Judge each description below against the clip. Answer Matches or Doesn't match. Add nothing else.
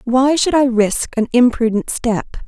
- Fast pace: Doesn't match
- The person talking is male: Doesn't match